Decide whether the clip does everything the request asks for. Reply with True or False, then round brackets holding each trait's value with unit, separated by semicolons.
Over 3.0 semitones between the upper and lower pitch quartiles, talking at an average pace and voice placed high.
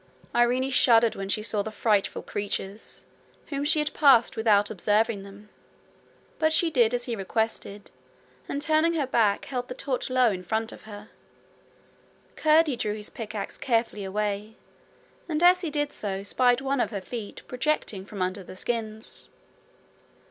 True (4.4 semitones; 160 wpm; 225 Hz)